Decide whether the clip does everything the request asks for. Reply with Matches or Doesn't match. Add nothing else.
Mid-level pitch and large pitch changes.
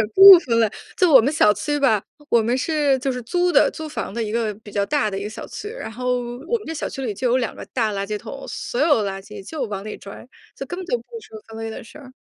Doesn't match